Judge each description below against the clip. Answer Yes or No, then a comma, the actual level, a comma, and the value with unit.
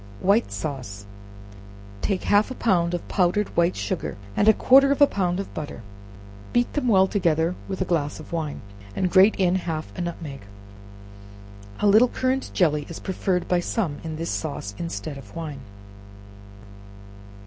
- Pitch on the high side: No, medium, 175 Hz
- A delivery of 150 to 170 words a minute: Yes, average, 160 wpm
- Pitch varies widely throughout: No, average, 4.3 semitones